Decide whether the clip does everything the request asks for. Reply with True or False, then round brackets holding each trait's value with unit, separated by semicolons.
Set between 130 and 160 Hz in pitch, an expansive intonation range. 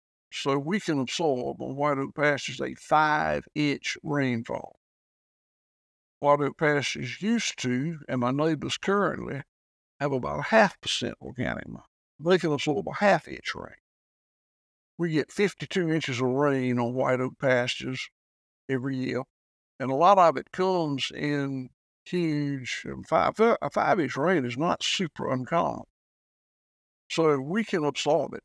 False (140 Hz; 4.0 semitones)